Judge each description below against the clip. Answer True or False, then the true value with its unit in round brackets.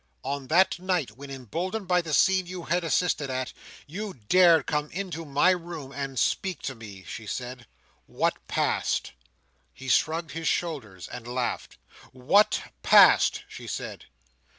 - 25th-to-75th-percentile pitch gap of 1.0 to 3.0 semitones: False (5.6 semitones)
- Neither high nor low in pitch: True (155 Hz)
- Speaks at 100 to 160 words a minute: True (150 wpm)